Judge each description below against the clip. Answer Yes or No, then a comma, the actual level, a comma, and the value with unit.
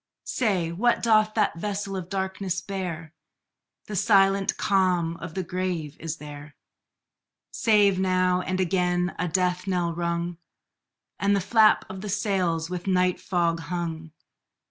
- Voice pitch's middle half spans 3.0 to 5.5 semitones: No, narrow, 2.5 semitones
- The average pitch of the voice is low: No, medium, 185 Hz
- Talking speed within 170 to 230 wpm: No, average, 140 wpm